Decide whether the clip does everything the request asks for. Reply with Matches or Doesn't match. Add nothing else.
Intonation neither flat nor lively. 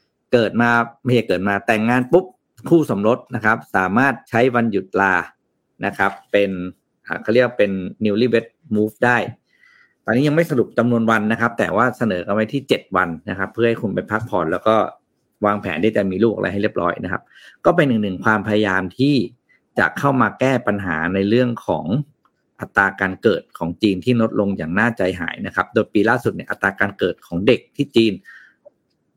Matches